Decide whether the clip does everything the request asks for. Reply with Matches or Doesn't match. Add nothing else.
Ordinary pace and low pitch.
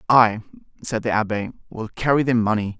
Matches